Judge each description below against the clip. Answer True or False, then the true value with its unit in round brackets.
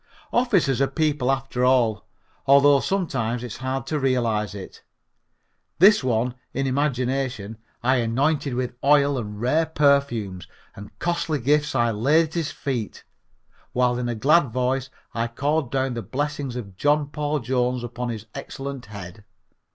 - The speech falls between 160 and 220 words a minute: False (150 wpm)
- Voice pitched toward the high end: False (130 Hz)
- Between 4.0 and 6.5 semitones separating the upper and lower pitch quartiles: False (3.4 semitones)